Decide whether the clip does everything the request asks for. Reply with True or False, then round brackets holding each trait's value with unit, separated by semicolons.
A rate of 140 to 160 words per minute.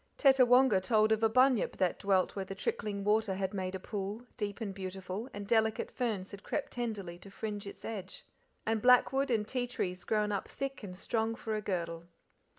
False (195 wpm)